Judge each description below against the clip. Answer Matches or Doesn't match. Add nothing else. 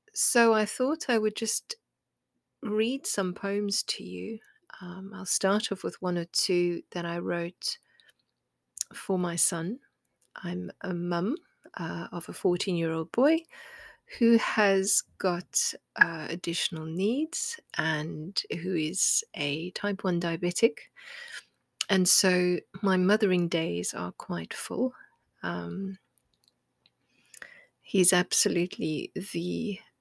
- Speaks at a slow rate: Matches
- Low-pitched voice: Doesn't match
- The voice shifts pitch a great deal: Doesn't match